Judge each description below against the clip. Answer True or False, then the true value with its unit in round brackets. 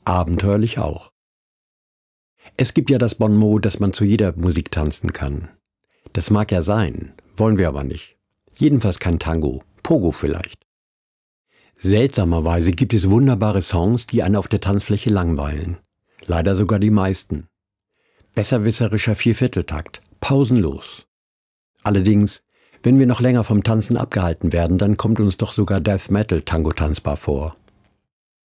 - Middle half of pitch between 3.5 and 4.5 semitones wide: True (4.2 semitones)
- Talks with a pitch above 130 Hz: False (100 Hz)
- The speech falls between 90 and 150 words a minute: True (135 wpm)